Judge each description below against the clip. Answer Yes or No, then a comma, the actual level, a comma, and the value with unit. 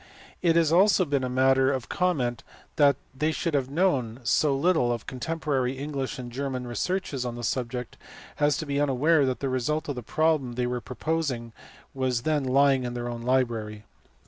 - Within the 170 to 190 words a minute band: Yes, average, 185 wpm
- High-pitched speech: No, low, 135 Hz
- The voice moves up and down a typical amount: Yes, average, 3.6 semitones